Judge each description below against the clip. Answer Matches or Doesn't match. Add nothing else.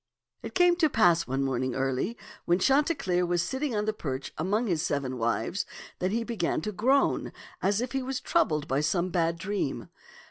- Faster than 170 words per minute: Matches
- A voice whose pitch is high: Doesn't match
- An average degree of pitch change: Doesn't match